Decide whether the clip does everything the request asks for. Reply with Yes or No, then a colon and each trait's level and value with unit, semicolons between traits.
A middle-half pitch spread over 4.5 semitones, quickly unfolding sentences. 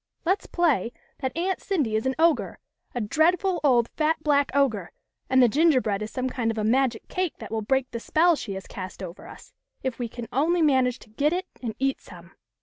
Yes: wide, 5.6 semitones; fast, 225 wpm